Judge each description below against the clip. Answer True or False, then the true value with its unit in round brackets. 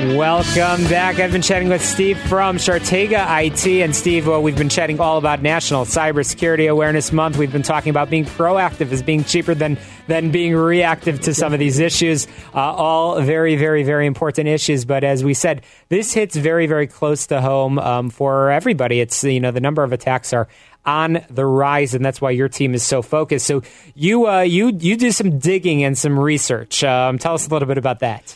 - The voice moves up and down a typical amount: True (3.4 semitones)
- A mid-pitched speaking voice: True (155 Hz)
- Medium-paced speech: False (210 wpm)